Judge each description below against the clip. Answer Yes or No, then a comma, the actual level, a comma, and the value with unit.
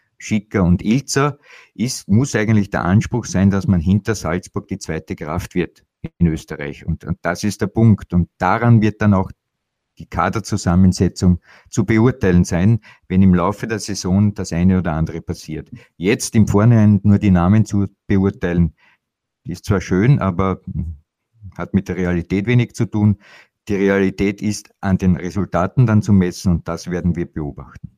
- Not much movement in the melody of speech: No, average, 3.2 semitones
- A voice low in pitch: Yes, very low, 95 Hz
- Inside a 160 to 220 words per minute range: Yes, average, 165 wpm